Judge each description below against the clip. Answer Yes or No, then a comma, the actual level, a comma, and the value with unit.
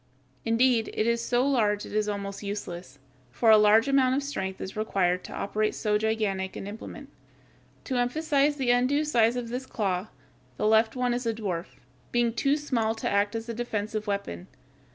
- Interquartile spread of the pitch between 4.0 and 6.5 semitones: No, average, 3.3 semitones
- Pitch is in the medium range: No, high, 225 Hz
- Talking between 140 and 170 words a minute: No, average, 190 wpm